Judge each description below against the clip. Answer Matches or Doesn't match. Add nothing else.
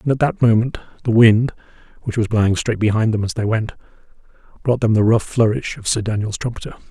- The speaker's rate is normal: Doesn't match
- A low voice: Matches